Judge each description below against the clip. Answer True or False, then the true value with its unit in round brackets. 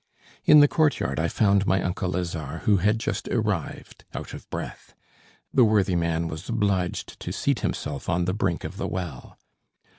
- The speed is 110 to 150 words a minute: False (175 wpm)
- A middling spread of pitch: True (3.9 semitones)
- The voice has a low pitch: True (95 Hz)